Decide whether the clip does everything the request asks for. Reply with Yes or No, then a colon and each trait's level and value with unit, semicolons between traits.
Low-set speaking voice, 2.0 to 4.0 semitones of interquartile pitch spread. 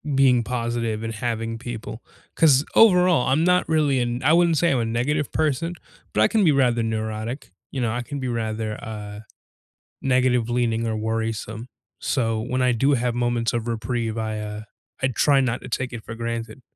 Yes: low, 120 Hz; average, 2.9 semitones